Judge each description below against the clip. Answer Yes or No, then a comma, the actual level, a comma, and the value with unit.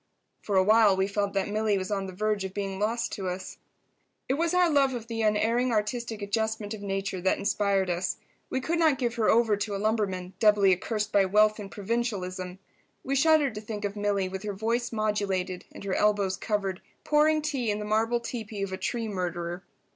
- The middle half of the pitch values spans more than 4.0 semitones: No, average, 2.9 semitones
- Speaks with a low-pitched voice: No, high, 210 Hz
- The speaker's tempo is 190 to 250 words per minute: Yes, fast, 205 wpm